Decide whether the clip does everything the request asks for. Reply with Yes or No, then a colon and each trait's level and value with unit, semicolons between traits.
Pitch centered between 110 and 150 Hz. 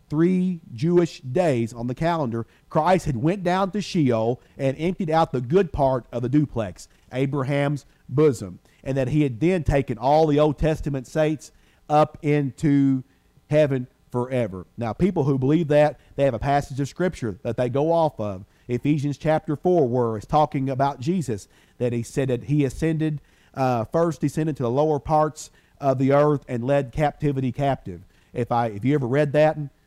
Yes: medium, 140 Hz